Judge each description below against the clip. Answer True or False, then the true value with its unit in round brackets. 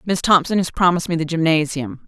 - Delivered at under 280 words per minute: True (200 wpm)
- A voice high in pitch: False (170 Hz)